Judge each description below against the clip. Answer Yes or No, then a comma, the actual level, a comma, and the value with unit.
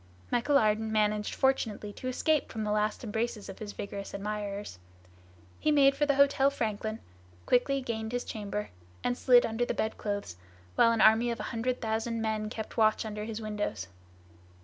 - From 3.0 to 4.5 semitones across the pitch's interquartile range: No, narrow, 2.6 semitones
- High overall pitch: Yes, high, 220 Hz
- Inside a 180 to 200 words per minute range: No, average, 170 wpm